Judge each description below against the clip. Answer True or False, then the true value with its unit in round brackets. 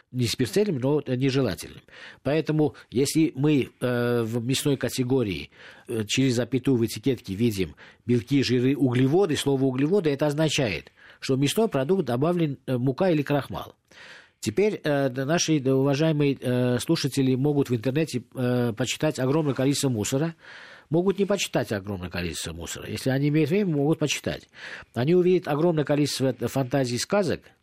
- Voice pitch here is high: False (135 Hz)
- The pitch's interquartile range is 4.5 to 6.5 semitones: False (3.7 semitones)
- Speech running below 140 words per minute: False (145 wpm)